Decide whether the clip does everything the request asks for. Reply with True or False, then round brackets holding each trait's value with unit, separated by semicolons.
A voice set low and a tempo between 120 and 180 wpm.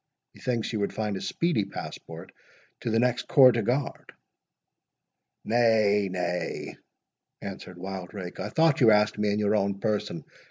True (105 Hz; 150 wpm)